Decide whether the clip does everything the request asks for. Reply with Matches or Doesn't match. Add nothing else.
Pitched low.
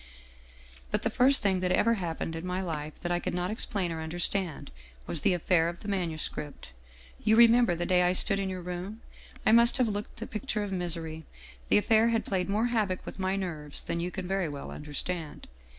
Doesn't match